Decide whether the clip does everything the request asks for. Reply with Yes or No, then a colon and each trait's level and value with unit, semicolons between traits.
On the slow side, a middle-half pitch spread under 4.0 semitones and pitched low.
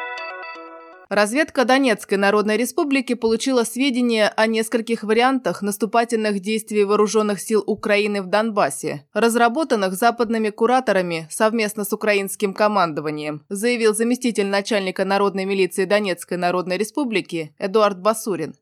No: slow, 105 wpm; average, 2.7 semitones; high, 210 Hz